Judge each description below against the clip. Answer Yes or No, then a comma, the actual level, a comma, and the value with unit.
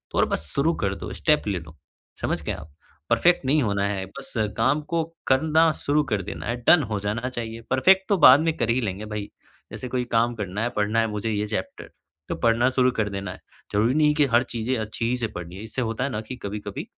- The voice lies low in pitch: Yes, low, 115 Hz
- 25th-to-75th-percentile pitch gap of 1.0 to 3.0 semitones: No, average, 4.3 semitones